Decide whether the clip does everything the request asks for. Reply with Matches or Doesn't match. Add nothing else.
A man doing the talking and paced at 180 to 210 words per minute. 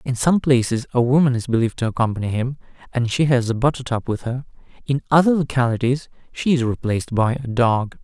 Matches